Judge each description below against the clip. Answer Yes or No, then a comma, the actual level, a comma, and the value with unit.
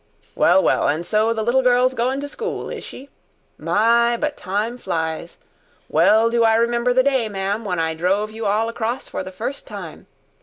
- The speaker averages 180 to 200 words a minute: Yes, average, 190 wpm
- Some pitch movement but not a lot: Yes, average, 3.5 semitones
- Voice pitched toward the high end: Yes, high, 225 Hz